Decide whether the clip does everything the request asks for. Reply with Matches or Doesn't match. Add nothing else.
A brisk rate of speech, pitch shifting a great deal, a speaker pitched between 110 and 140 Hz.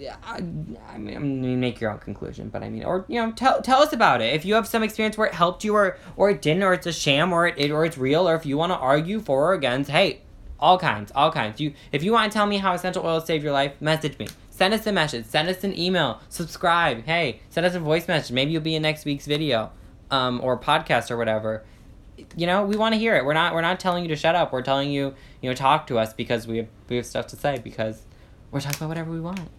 Doesn't match